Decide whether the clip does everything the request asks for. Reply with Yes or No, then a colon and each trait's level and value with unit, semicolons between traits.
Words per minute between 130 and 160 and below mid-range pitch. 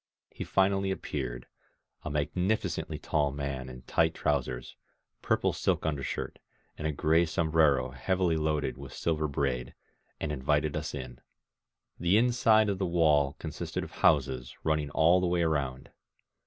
Yes: average, 155 wpm; very low, 75 Hz